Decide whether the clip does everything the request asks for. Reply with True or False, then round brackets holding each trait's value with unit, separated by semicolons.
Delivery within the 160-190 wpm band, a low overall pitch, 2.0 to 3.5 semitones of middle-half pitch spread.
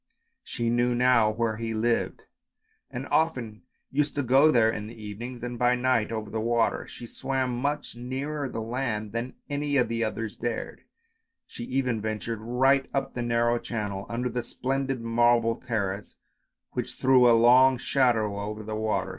True (170 wpm; 120 Hz; 2.5 semitones)